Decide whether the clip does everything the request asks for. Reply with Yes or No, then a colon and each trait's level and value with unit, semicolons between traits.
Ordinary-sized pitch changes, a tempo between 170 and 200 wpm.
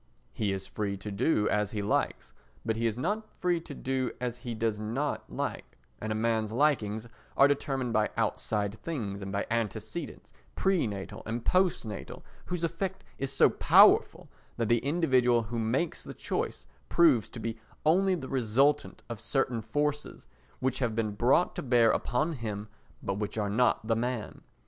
Yes: average, 4.7 semitones; average, 175 wpm